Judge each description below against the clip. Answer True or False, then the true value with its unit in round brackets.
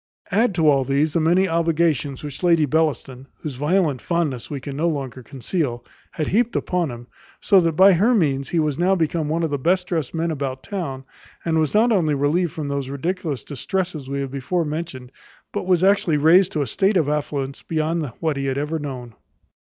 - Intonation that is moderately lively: True (3.8 semitones)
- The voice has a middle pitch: True (155 Hz)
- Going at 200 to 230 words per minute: True (205 wpm)